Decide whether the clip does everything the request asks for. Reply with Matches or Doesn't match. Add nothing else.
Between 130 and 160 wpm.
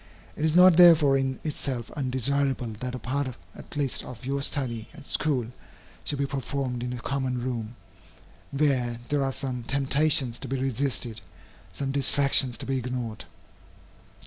Matches